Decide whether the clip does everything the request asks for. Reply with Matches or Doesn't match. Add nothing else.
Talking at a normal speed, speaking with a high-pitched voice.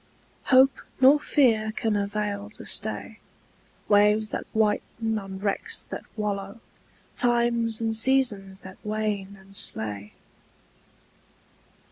Doesn't match